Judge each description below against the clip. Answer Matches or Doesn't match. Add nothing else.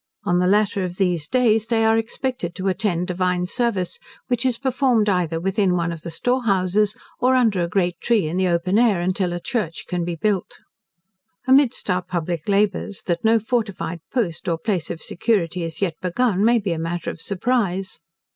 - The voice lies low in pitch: Doesn't match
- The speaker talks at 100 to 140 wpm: Doesn't match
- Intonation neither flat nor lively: Matches